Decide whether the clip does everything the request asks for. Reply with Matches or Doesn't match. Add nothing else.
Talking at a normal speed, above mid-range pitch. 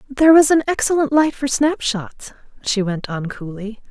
Matches